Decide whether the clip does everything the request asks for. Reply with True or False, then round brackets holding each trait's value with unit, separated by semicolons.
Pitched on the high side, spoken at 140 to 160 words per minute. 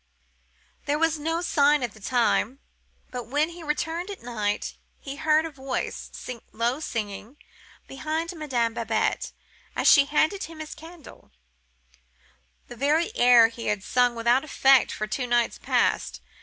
True (275 Hz; 145 wpm)